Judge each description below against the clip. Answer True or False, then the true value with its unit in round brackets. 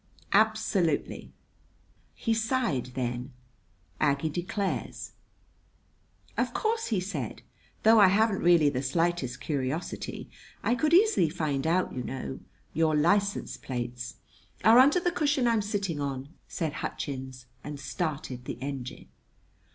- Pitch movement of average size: False (8.1 semitones)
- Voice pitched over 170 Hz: False (160 Hz)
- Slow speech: True (125 wpm)